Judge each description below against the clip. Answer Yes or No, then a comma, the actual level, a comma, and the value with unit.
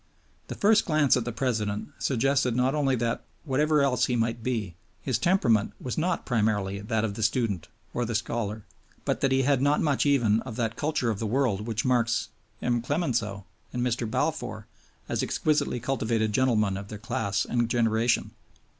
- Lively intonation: No, average, 3.3 semitones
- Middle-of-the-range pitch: No, low, 120 Hz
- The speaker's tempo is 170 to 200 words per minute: Yes, average, 180 wpm